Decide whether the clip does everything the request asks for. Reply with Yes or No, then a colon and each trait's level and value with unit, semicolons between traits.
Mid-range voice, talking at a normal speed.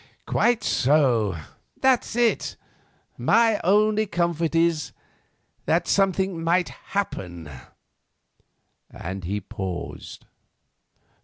No: medium, 170 Hz; slow, 75 wpm